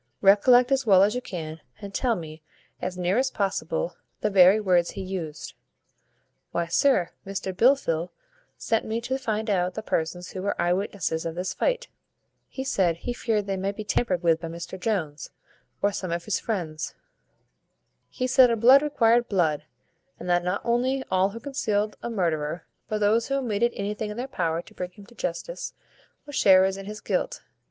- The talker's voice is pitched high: Yes, high, 200 Hz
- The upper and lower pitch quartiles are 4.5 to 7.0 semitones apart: Yes, average, 4.8 semitones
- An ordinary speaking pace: Yes, average, 185 wpm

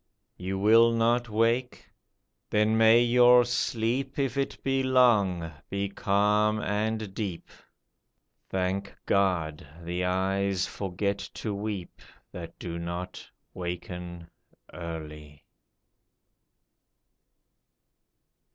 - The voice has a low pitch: Yes, low, 100 Hz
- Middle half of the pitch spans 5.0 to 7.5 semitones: No, average, 4.3 semitones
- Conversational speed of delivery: No, slow, 90 wpm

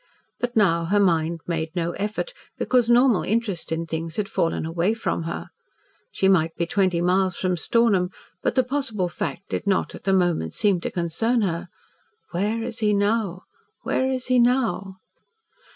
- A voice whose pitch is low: No, high, 195 Hz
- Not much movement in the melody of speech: No, average, 5.0 semitones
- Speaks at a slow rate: No, average, 170 wpm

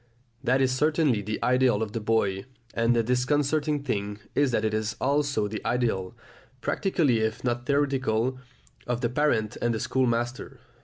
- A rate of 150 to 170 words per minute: Yes, average, 160 wpm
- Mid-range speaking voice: No, low, 120 Hz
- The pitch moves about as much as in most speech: Yes, average, 3.9 semitones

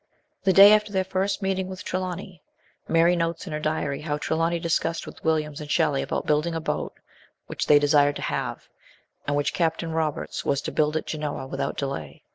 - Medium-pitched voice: Yes, medium, 160 Hz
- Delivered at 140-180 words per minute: No, average, 195 wpm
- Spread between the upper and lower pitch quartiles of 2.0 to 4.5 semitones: Yes, average, 3.2 semitones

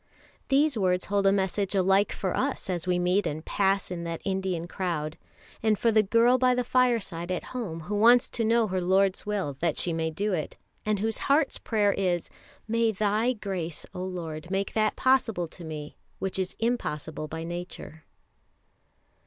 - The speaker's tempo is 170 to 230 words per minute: Yes, average, 180 wpm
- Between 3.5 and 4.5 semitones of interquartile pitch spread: Yes, average, 4.1 semitones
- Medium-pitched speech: No, high, 195 Hz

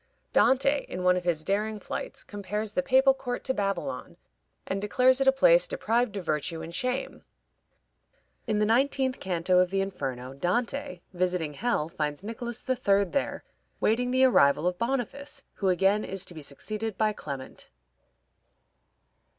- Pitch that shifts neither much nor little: No, wide, 6.0 semitones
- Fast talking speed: No, average, 155 wpm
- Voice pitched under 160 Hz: No, high, 210 Hz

